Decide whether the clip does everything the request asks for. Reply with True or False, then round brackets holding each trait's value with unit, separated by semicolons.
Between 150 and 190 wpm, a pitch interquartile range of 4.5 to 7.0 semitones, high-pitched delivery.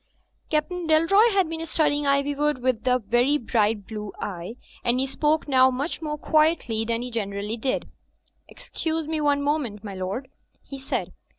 True (165 wpm; 5.2 semitones; 270 Hz)